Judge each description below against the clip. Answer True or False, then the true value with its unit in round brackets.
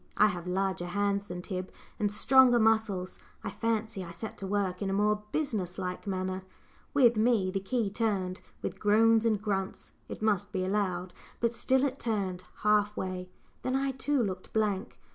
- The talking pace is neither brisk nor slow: True (180 wpm)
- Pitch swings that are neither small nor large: True (3.1 semitones)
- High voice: True (205 Hz)